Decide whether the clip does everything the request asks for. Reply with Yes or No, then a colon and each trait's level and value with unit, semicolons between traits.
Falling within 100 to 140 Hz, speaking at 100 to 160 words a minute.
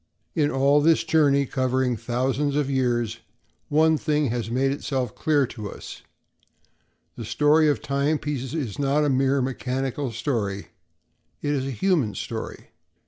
Yes: low, 135 Hz; average, 140 wpm